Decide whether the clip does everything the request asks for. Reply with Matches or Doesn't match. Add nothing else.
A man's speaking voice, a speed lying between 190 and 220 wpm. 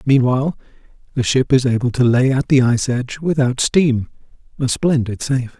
Doesn't match